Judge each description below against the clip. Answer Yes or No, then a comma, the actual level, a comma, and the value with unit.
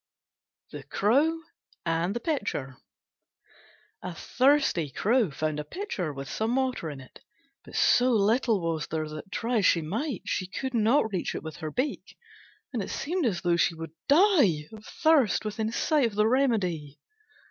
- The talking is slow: No, average, 170 wpm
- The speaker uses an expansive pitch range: Yes, wide, 7.9 semitones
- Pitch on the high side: Yes, high, 215 Hz